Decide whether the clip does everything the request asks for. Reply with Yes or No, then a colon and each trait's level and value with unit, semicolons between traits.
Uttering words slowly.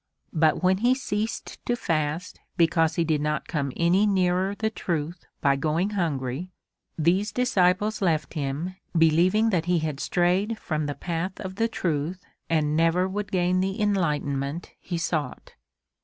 No: average, 155 wpm